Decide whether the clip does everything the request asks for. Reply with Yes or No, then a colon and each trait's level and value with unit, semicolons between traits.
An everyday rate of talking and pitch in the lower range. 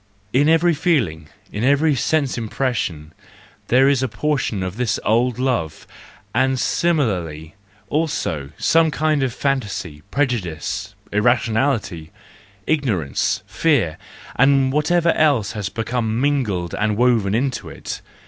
No: slow, 120 wpm; low, 125 Hz